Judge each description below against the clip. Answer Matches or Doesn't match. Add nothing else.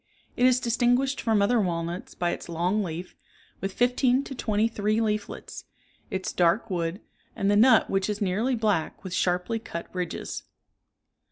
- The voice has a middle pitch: Doesn't match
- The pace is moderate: Matches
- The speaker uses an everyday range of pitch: Matches